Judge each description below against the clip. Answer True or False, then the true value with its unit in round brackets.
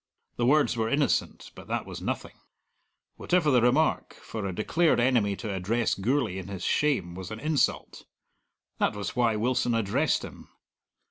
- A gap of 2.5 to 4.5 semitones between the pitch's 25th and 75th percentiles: False (5.4 semitones)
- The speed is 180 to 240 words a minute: False (160 wpm)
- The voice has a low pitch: True (120 Hz)